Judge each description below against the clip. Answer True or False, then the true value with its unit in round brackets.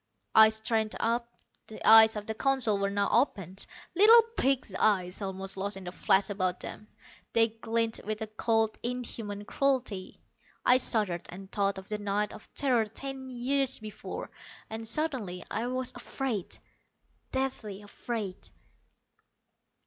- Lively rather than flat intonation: False (3.6 semitones)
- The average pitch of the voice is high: True (220 Hz)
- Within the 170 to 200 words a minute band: False (140 wpm)